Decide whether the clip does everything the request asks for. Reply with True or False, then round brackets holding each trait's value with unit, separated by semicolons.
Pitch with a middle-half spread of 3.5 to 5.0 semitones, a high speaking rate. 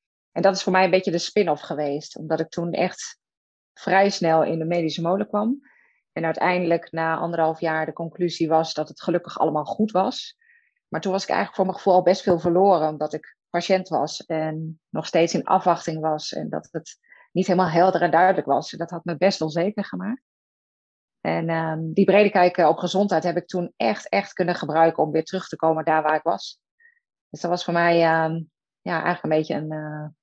False (2.8 semitones; 215 wpm)